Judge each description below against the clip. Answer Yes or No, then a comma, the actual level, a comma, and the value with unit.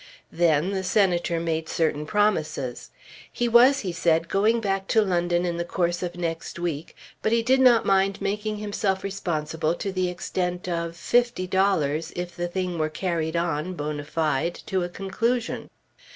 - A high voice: No, medium, 175 Hz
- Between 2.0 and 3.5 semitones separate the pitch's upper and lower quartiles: Yes, average, 3.0 semitones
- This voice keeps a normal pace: Yes, average, 165 wpm